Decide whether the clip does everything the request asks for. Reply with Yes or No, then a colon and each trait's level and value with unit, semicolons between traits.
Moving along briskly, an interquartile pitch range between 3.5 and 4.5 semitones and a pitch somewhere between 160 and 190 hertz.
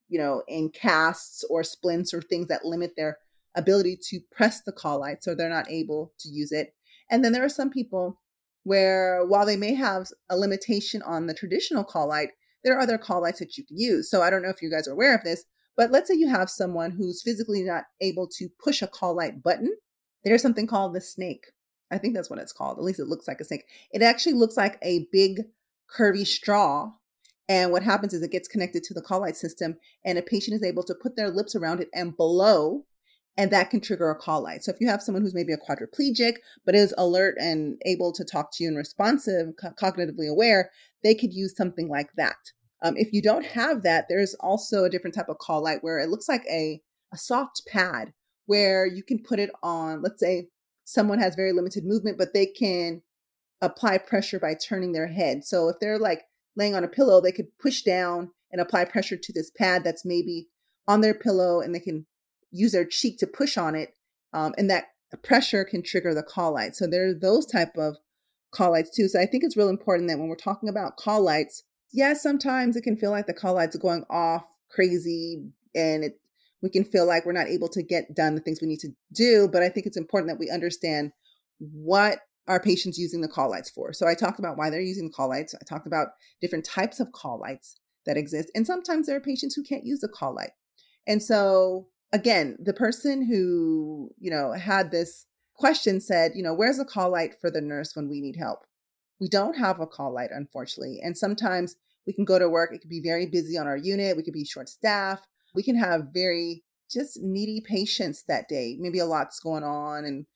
Yes: fast, 230 wpm; average, 4.0 semitones; medium, 185 Hz